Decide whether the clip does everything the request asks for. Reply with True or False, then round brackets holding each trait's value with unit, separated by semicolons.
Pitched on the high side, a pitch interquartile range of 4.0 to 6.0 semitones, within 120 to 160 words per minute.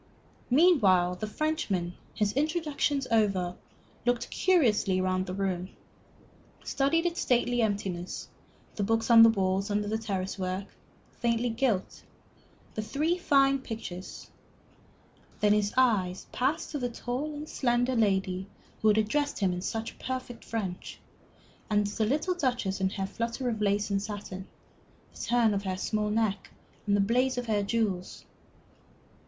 True (220 Hz; 4.4 semitones; 150 wpm)